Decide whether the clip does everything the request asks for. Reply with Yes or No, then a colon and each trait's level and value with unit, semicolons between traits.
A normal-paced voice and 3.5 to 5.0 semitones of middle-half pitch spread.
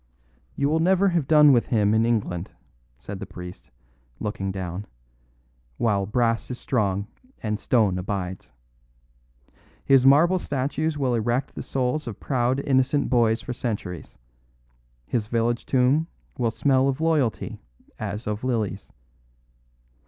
No: slow, 130 wpm; average, 4.7 semitones